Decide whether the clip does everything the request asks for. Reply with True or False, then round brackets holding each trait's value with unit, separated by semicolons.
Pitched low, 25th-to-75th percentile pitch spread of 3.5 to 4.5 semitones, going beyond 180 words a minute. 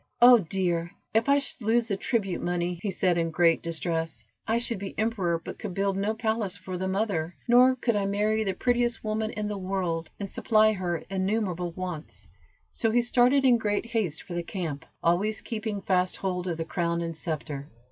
False (195 Hz; 4.2 semitones; 200 wpm)